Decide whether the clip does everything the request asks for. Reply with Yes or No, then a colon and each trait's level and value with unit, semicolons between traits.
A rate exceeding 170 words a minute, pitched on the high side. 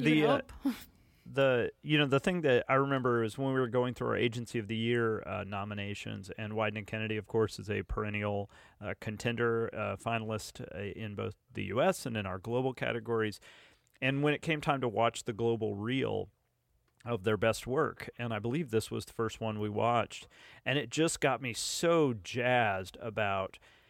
No: average, 195 wpm; low, 115 Hz